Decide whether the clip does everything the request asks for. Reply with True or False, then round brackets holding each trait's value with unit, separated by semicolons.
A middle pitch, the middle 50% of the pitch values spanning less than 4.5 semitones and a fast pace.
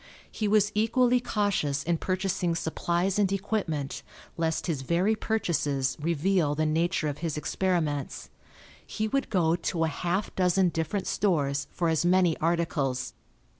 False (170 Hz; 3.9 semitones; 140 wpm)